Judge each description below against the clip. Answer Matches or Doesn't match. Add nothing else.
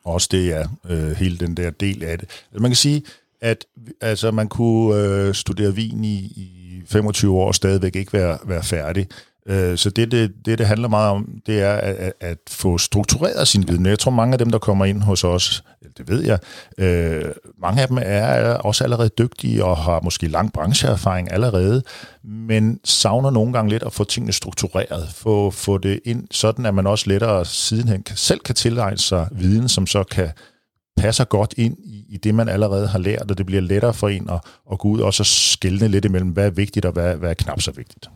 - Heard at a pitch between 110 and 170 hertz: Doesn't match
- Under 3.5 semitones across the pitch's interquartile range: Matches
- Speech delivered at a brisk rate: Doesn't match